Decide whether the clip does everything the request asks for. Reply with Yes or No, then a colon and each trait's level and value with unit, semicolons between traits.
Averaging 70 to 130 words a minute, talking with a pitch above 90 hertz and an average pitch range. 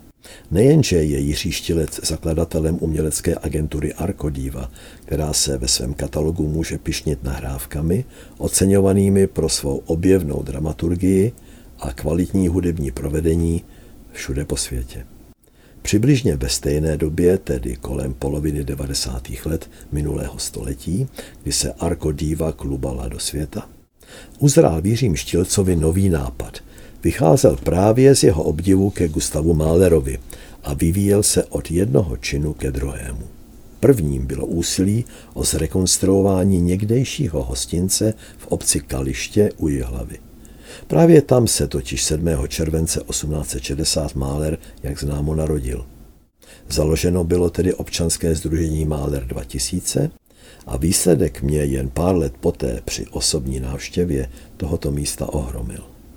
No: slow, 115 wpm; very low, 80 Hz; average, 4.2 semitones